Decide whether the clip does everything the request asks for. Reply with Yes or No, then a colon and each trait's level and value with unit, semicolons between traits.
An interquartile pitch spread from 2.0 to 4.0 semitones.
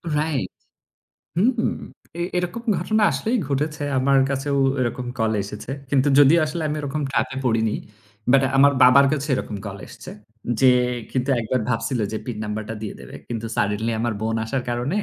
No: average, 4.7 semitones